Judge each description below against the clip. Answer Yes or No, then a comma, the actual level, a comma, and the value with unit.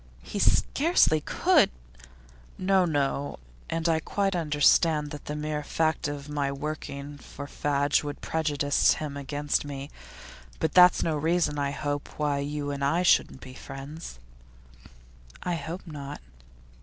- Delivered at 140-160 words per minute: Yes, average, 145 wpm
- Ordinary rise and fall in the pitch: No, narrow, 2.2 semitones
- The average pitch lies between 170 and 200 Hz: No, medium, 150 Hz